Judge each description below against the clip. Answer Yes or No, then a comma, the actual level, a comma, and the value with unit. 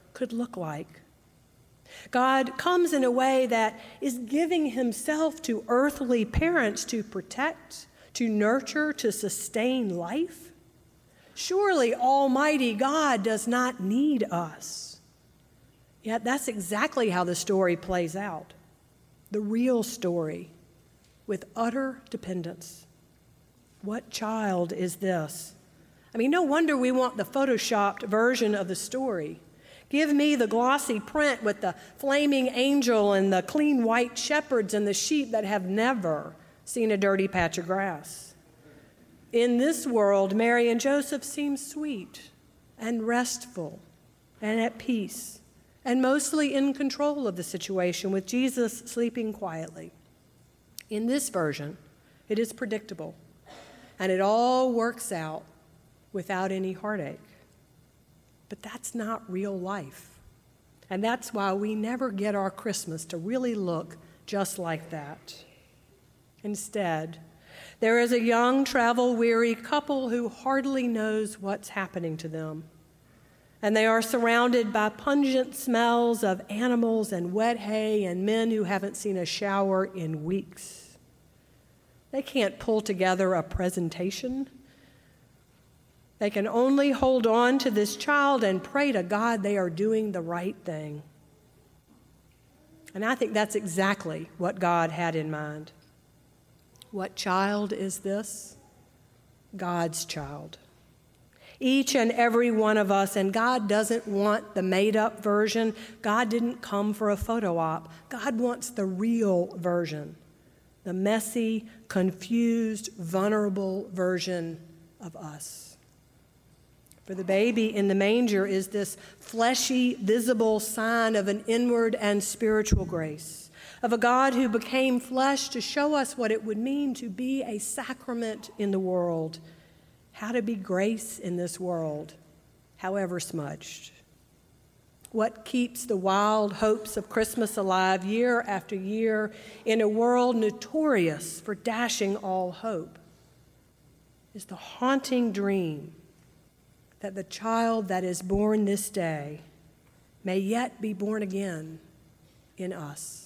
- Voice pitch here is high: Yes, high, 210 Hz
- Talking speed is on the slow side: Yes, slow, 130 wpm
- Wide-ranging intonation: No, average, 4.7 semitones